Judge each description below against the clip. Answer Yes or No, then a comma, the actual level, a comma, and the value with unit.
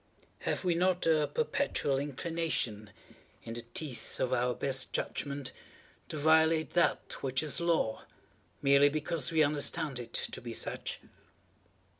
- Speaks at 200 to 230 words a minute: No, slow, 135 wpm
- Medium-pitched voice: Yes, medium, 145 Hz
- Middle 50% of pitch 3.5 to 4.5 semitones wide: Yes, average, 3.9 semitones